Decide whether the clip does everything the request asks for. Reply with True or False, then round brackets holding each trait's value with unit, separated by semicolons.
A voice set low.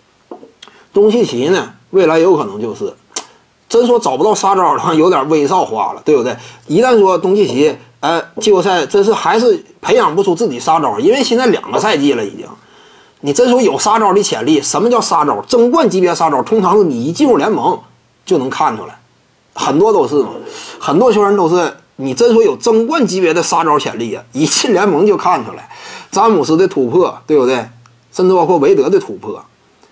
False (235 Hz)